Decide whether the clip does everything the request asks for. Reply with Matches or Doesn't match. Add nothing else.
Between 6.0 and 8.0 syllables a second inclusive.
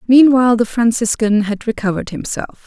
Doesn't match